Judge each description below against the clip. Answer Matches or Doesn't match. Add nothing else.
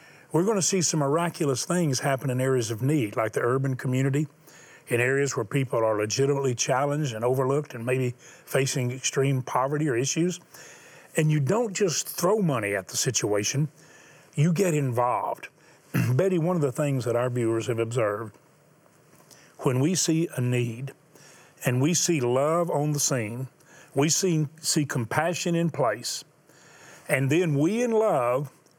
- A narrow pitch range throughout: Doesn't match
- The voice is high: Doesn't match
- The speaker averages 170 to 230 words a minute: Doesn't match